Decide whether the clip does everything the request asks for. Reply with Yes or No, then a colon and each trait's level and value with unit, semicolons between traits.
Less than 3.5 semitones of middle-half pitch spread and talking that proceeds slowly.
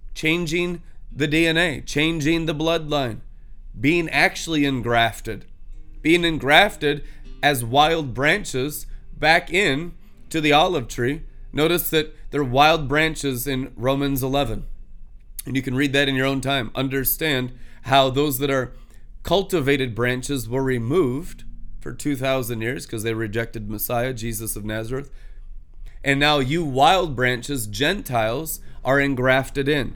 No: average, 4.0 semitones; slow, 130 wpm